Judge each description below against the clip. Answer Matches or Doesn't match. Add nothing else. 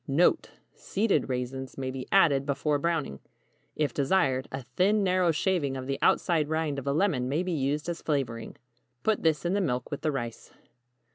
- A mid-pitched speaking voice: Matches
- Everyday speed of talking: Matches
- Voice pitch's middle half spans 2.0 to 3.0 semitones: Doesn't match